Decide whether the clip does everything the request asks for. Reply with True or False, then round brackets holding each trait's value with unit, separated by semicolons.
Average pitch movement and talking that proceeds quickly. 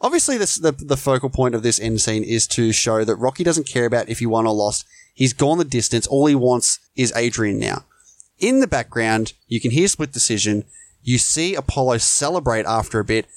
True (3.8 semitones; 215 wpm)